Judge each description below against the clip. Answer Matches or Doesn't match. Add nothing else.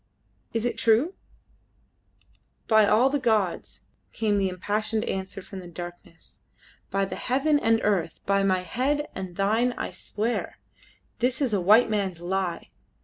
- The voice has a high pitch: Matches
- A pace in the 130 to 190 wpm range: Matches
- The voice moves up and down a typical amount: Matches